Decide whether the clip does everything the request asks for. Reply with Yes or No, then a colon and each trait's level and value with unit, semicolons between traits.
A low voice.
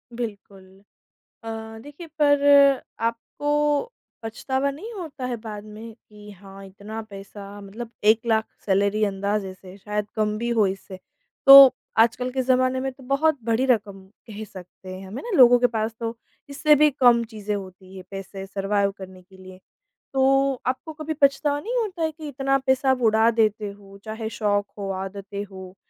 No: high, 220 Hz